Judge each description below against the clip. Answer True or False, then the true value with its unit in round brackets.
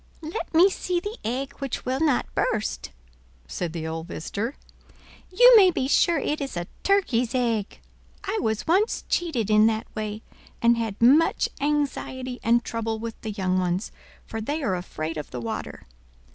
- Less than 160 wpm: False (170 wpm)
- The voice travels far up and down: True (6.0 semitones)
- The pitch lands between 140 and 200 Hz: False (235 Hz)